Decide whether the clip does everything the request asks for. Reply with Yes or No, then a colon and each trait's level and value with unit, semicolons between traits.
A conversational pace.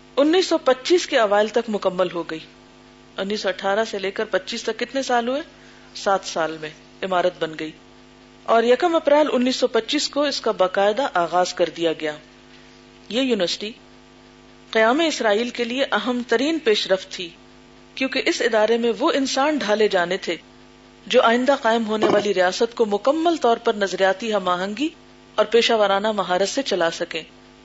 Yes: average, 175 wpm